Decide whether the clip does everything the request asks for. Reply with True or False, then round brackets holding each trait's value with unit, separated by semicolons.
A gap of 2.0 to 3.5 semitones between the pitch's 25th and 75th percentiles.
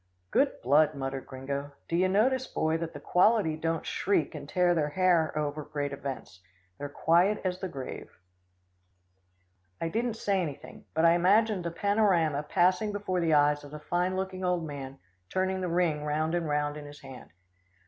False (4.1 semitones)